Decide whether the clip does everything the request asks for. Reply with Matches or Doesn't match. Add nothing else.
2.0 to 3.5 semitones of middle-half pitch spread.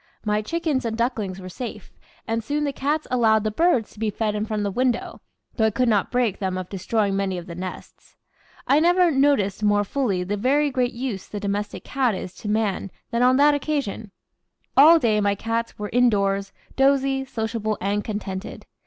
Doesn't match